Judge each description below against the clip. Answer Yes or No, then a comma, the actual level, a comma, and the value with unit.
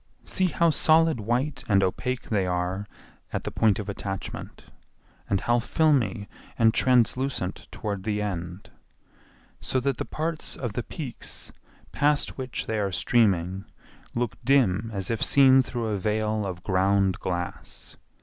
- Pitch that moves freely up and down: No, average, 5.0 semitones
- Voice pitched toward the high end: No, low, 110 Hz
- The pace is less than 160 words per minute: Yes, average, 145 wpm